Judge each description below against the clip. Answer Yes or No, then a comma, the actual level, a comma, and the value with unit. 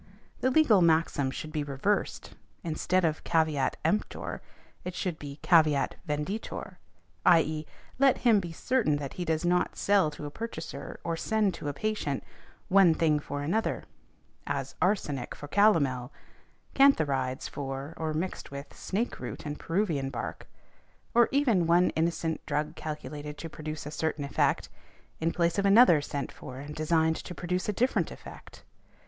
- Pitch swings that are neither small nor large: Yes, average, 4.3 semitones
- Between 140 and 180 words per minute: Yes, average, 155 wpm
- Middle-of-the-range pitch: Yes, medium, 160 Hz